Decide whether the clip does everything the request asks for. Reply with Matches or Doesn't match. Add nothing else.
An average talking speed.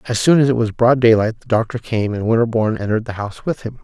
Doesn't match